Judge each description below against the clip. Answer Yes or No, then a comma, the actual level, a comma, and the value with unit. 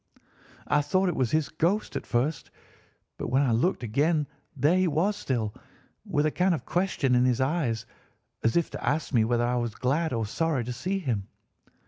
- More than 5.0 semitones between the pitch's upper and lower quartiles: Yes, wide, 5.6 semitones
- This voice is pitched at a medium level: Yes, medium, 145 Hz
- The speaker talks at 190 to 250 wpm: Yes, average, 195 wpm